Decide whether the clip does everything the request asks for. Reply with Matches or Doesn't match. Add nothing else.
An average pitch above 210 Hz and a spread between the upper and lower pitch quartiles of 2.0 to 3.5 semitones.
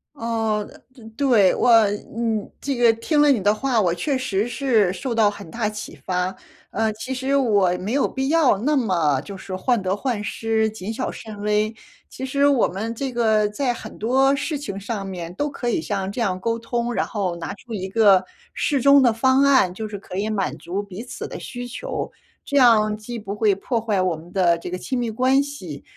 Doesn't match